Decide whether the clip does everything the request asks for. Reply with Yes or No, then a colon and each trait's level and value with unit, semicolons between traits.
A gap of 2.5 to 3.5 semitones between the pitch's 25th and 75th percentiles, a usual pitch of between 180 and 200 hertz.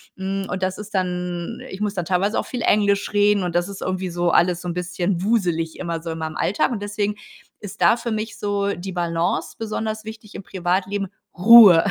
Yes: average, 2.9 semitones; high, 190 Hz